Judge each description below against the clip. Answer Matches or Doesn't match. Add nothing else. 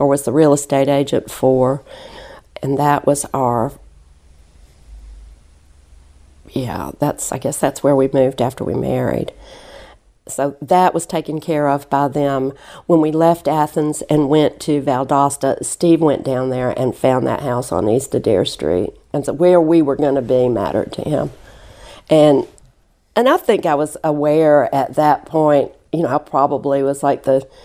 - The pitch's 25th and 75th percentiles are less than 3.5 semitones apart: Matches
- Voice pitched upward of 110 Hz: Matches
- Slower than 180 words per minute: Matches